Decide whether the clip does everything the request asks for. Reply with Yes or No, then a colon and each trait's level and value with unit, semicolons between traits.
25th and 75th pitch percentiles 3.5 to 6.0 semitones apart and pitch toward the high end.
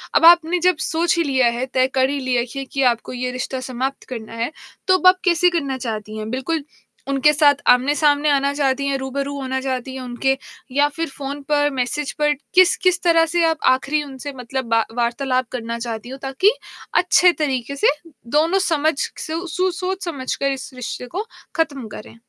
Yes: average, 3.9 semitones; very high, 275 Hz